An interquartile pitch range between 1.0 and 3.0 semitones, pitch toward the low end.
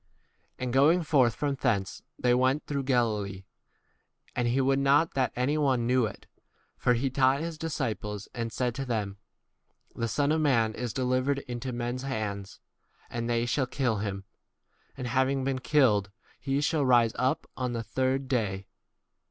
Yes: average, 2.7 semitones; low, 125 Hz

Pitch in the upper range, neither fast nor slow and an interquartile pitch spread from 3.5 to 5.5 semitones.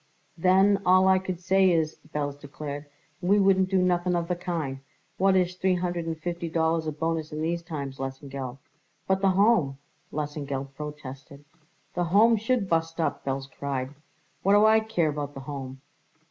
No: medium, 165 Hz; average, 175 wpm; average, 4.5 semitones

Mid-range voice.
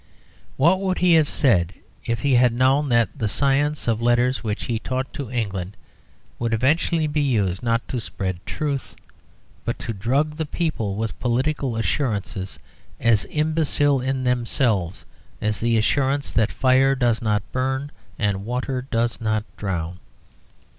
No: low, 125 Hz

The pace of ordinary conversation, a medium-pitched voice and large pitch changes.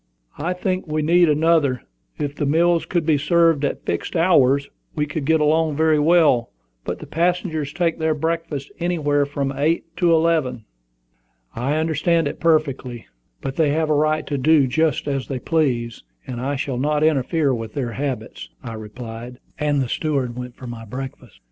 No: average, 175 wpm; medium, 150 Hz; average, 3.6 semitones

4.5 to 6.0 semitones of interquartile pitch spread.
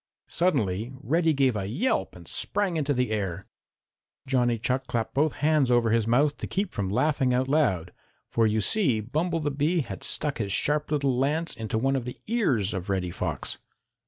Yes: wide, 5.5 semitones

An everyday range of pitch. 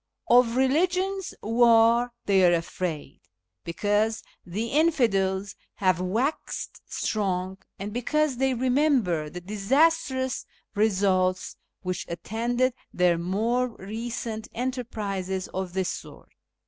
Yes: average, 5.0 semitones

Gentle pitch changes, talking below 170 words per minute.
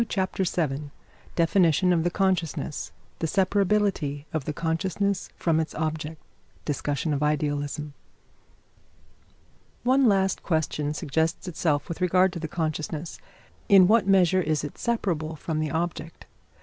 No: average, 3.6 semitones; slow, 135 wpm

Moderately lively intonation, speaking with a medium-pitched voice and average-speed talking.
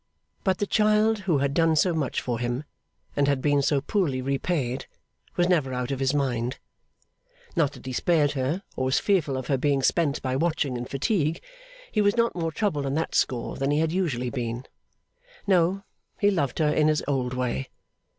Yes: average, 4.7 semitones; medium, 145 Hz; average, 195 wpm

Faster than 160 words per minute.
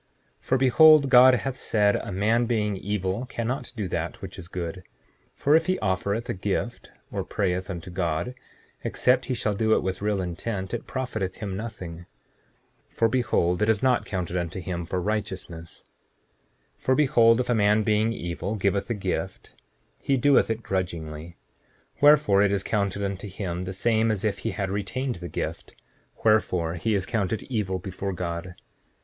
Yes: average, 180 wpm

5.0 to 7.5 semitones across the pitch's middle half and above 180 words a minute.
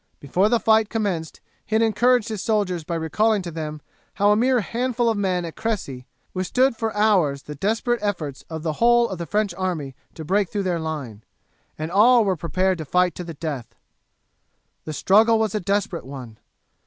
Yes: wide, 5.4 semitones; average, 195 wpm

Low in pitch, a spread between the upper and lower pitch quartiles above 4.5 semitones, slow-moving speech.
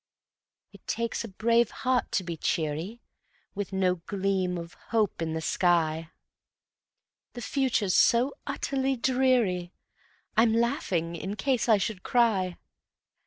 No: high, 205 Hz; average, 5.1 semitones; slow, 125 wpm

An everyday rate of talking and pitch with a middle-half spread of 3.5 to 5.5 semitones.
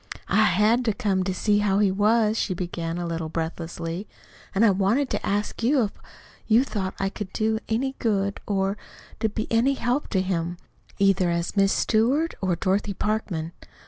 No: average, 180 wpm; average, 3.0 semitones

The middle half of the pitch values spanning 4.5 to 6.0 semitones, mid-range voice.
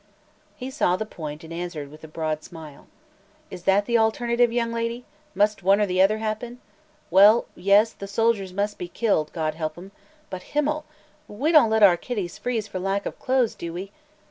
No: average, 4.9 semitones; high, 200 Hz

